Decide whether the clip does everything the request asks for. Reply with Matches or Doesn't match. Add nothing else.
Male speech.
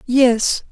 Matches